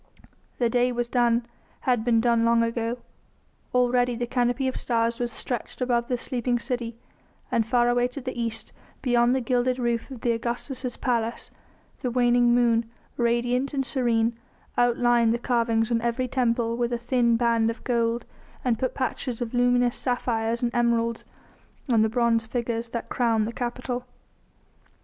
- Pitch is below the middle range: No, high, 240 Hz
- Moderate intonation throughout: No, narrow, 1.1 semitones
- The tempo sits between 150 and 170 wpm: Yes, average, 165 wpm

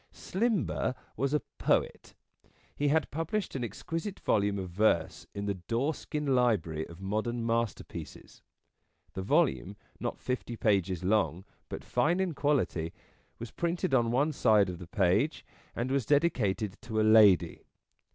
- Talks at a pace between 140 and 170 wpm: Yes, average, 145 wpm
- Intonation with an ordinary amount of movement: No, wide, 6.5 semitones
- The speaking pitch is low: Yes, low, 115 Hz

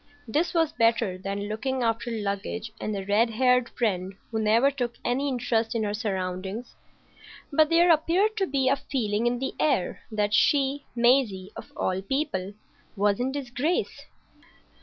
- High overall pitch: Yes, high, 235 Hz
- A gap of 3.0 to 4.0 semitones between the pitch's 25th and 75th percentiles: No, average, 4.8 semitones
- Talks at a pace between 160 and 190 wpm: No, average, 150 wpm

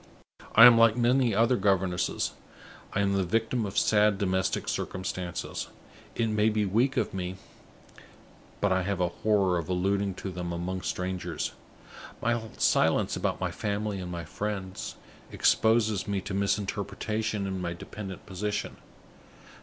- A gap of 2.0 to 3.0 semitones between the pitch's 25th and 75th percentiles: Yes, narrow, 2.5 semitones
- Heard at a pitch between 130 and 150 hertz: No, low, 100 Hz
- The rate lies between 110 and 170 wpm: Yes, average, 145 wpm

